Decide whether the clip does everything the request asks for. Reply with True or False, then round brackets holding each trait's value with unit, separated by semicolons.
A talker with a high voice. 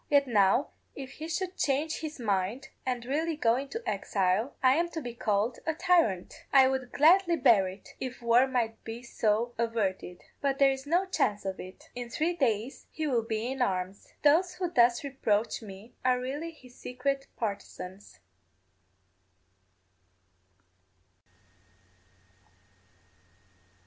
True (250 Hz)